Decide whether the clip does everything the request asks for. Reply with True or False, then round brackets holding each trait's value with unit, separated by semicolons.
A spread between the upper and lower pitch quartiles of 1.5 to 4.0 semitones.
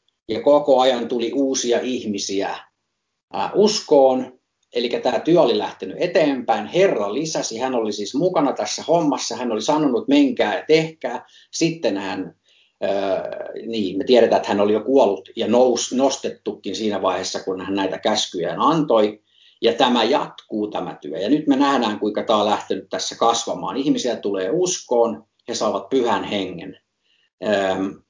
False (5.0 semitones)